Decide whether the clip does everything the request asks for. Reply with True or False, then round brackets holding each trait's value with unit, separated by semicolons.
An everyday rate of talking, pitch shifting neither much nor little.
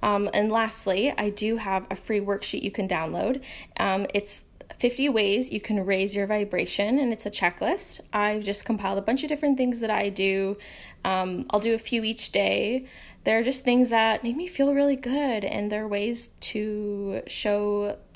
True (190 wpm; 3.3 semitones)